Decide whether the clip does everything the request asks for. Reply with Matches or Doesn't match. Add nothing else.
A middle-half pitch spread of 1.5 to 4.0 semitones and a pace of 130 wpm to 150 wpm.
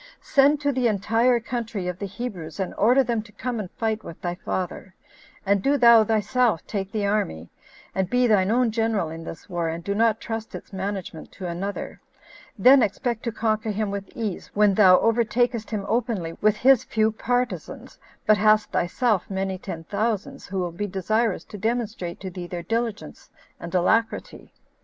Doesn't match